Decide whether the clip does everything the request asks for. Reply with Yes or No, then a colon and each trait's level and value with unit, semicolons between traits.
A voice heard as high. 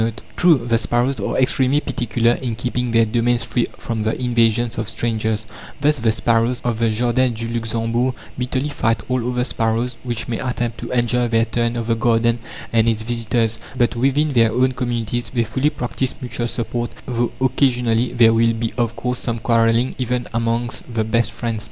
No: low, 120 Hz